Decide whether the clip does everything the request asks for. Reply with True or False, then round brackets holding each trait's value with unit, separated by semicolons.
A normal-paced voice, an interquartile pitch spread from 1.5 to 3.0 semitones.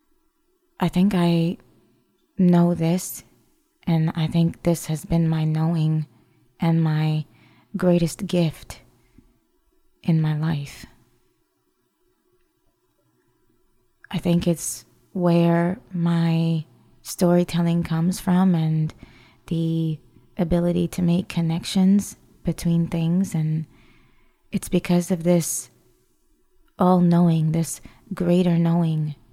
False (95 wpm; 2.6 semitones)